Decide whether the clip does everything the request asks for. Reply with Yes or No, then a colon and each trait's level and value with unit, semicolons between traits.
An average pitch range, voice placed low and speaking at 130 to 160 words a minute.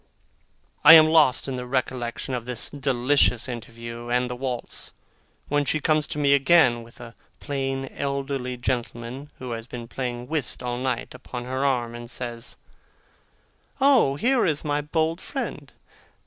Yes: average, 3.1 semitones; low, 130 Hz; average, 155 wpm